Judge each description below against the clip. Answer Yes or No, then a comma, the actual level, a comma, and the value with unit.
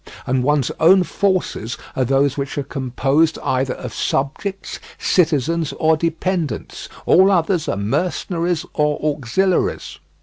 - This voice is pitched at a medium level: Yes, medium, 155 Hz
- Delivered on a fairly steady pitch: No, average, 4.8 semitones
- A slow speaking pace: Yes, slow, 125 wpm